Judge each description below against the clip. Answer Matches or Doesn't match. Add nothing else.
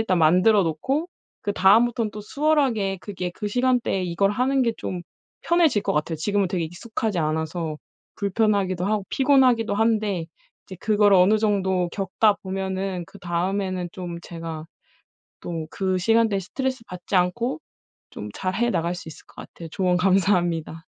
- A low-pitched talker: Doesn't match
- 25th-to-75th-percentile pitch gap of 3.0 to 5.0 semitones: Matches